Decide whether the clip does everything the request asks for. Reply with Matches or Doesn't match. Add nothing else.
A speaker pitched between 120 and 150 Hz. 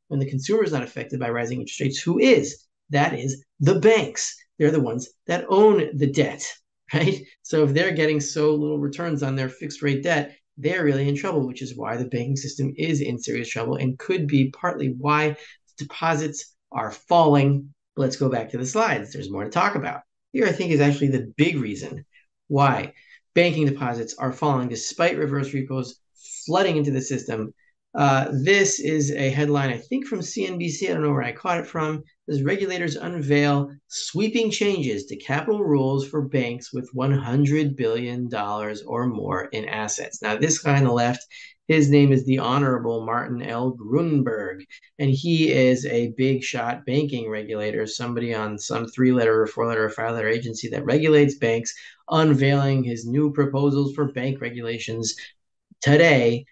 Matches